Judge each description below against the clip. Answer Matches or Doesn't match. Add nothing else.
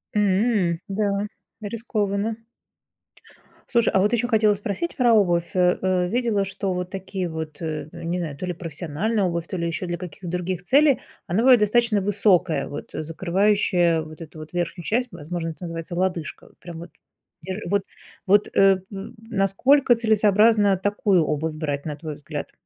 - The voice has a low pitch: Doesn't match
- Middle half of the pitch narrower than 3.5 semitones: Doesn't match